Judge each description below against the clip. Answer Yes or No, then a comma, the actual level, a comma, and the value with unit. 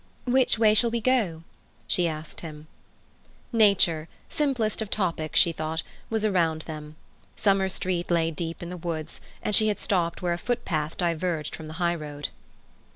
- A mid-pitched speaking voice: Yes, medium, 175 Hz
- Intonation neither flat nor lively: Yes, average, 4.8 semitones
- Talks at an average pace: Yes, average, 155 wpm